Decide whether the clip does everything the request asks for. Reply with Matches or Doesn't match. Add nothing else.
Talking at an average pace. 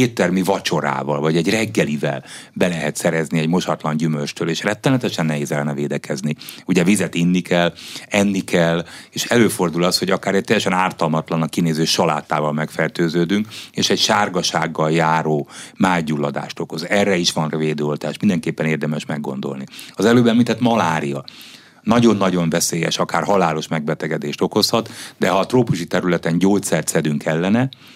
Matches